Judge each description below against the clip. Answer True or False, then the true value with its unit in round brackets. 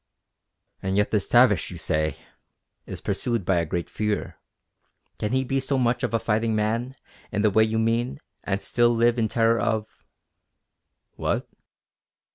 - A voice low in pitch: True (110 Hz)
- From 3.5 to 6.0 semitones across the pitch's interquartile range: False (2.5 semitones)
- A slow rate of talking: False (160 wpm)